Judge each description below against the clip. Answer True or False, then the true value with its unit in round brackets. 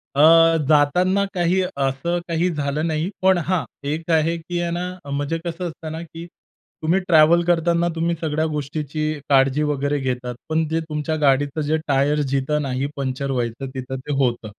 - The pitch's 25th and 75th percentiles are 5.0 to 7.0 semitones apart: False (3.3 semitones)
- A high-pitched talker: False (155 Hz)